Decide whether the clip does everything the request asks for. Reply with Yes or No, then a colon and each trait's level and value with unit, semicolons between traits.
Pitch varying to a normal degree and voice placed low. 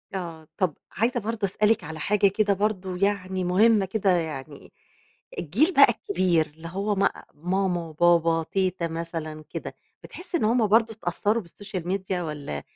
No: average, 4.0 semitones; medium, 185 Hz